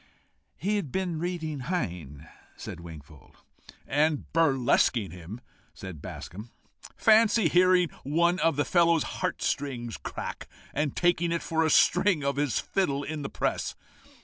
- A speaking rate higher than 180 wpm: No, average, 140 wpm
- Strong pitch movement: Yes, wide, 6.3 semitones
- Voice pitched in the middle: Yes, medium, 150 Hz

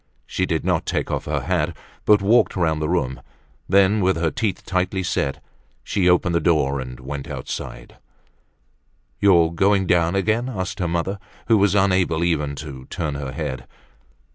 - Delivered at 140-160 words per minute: No, average, 170 wpm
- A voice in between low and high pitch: No, very low, 85 Hz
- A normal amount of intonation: Yes, average, 4.3 semitones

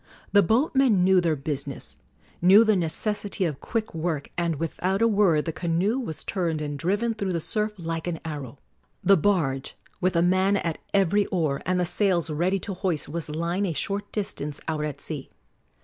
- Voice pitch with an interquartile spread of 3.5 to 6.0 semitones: Yes, average, 4.1 semitones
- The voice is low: No, medium, 175 Hz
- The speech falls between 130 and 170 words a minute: No, average, 185 wpm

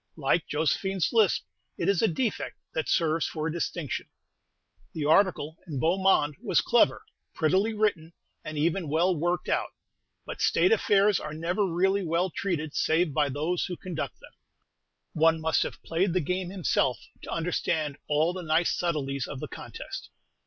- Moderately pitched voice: Yes, medium, 165 Hz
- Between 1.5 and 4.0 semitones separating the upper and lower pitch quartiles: Yes, average, 3.2 semitones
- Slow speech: No, average, 165 wpm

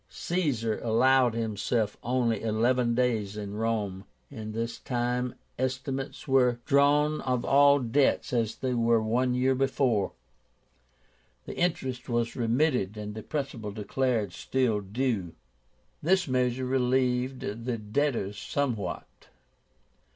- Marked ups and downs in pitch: No, average, 3.0 semitones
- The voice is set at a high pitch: No, low, 125 Hz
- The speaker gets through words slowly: Yes, slow, 115 wpm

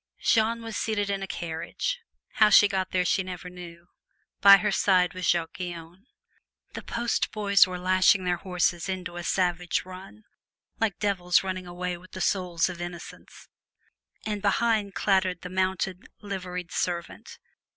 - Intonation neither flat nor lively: No, narrow, 2.0 semitones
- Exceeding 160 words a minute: No, average, 155 wpm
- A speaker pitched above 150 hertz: Yes, medium, 185 Hz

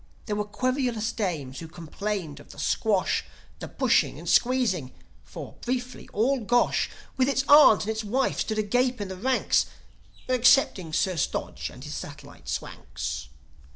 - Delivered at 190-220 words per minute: No, average, 155 wpm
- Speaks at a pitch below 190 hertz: No, high, 215 Hz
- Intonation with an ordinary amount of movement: No, wide, 6.5 semitones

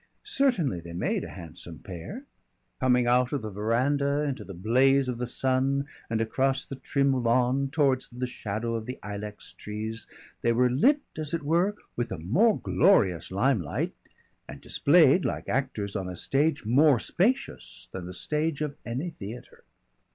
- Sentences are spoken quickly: No, average, 165 wpm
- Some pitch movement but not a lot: Yes, average, 4.9 semitones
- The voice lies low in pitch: Yes, low, 125 Hz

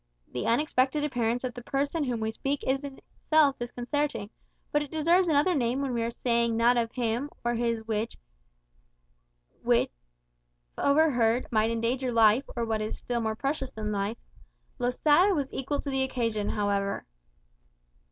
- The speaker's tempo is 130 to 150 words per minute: No, average, 160 wpm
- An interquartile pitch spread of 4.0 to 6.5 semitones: No, average, 3.6 semitones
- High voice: Yes, high, 245 Hz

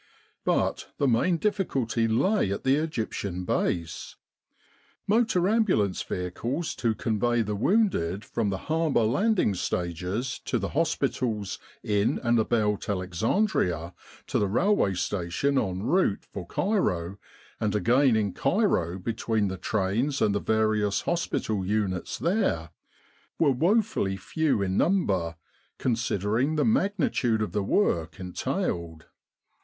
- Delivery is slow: Yes, slow, 125 wpm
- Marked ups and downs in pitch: Yes, wide, 8.0 semitones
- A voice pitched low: Yes, low, 110 Hz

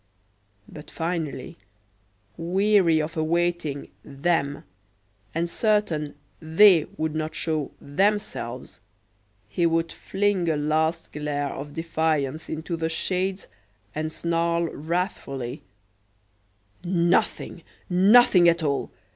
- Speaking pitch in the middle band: Yes, medium, 165 Hz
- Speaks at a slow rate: Yes, slow, 95 wpm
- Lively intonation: No, narrow, 2.4 semitones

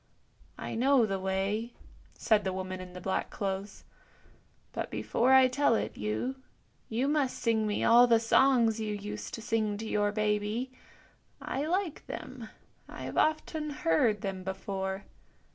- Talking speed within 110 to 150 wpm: No, average, 160 wpm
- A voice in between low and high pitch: No, high, 220 Hz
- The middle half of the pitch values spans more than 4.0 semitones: Yes, average, 4.6 semitones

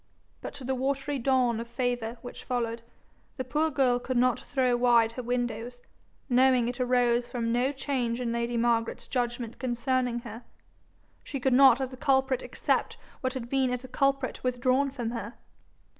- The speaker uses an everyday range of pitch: No, narrow, 1.6 semitones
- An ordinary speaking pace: Yes, average, 175 wpm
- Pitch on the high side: Yes, very high, 250 Hz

